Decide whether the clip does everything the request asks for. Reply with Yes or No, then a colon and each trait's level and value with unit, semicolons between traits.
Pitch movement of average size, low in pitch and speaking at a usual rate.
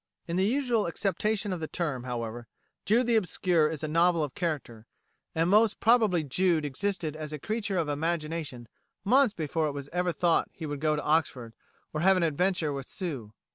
No: average, 4.4 semitones; medium, 165 Hz; average, 190 wpm